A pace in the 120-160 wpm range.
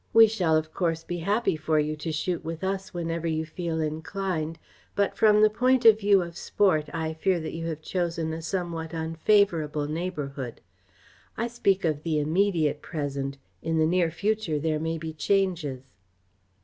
No: average, 175 wpm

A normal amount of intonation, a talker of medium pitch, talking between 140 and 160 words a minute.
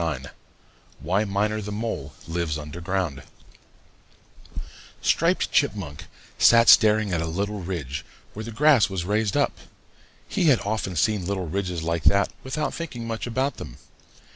No: average, 4.7 semitones; low, 100 Hz; average, 145 wpm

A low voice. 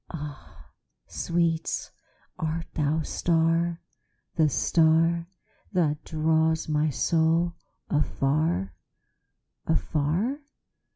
No: medium, 160 Hz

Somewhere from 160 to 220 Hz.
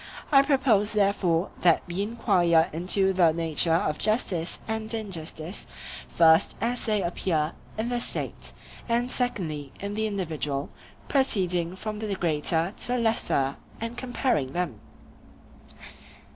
Yes: high, 190 Hz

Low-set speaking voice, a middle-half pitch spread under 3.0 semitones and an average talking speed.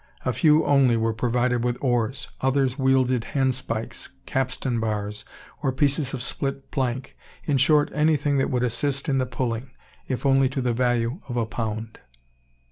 Yes: low, 130 Hz; narrow, 2.4 semitones; average, 160 wpm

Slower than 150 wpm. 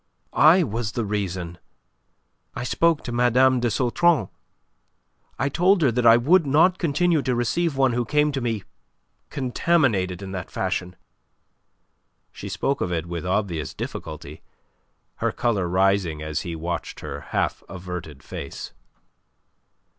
Yes: average, 140 wpm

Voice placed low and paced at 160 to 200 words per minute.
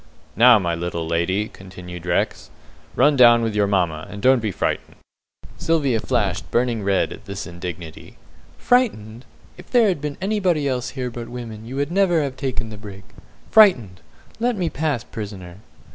Yes: low, 115 Hz; average, 165 wpm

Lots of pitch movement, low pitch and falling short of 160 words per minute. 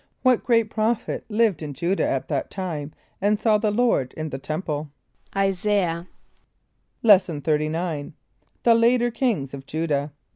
No: wide, 6.2 semitones; medium, 185 Hz; average, 150 wpm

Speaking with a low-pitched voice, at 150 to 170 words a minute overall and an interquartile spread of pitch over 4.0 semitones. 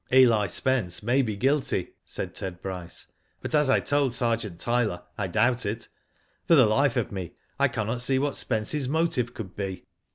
No: low, 115 Hz; average, 185 wpm; average, 4.7 semitones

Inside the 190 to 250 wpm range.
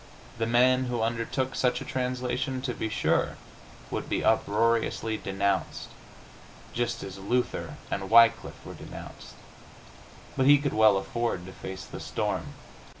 No: average, 140 wpm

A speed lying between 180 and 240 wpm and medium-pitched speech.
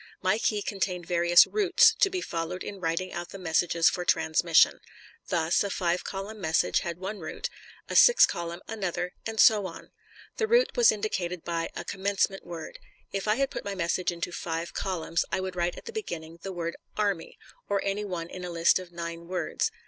Yes: average, 195 wpm; medium, 180 Hz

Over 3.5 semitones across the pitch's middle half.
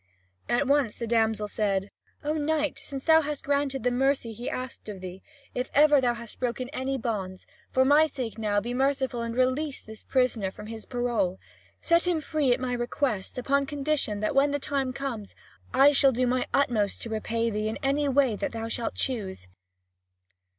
Yes: average, 3.9 semitones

